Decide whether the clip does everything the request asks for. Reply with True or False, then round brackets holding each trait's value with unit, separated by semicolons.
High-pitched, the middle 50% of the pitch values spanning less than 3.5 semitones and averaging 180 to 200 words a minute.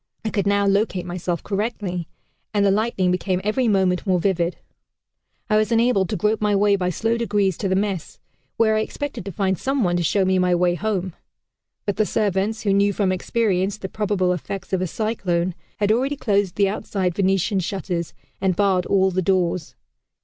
True (195 Hz; 2.5 semitones; 195 wpm)